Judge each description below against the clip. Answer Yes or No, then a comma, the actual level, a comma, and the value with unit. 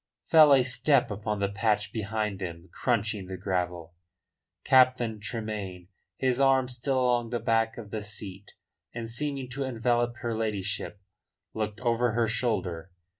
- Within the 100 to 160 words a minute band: Yes, average, 145 wpm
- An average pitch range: Yes, average, 3.4 semitones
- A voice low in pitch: Yes, low, 110 Hz